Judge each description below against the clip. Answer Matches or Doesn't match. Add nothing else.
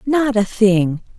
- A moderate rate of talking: Matches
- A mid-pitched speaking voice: Doesn't match